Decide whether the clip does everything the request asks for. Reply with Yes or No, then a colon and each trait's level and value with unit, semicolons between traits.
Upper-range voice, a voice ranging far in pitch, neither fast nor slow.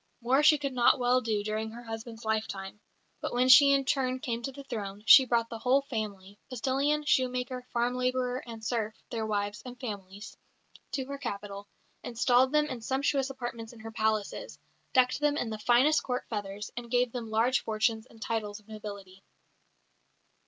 No: high, 235 Hz; average, 3.0 semitones; average, 180 wpm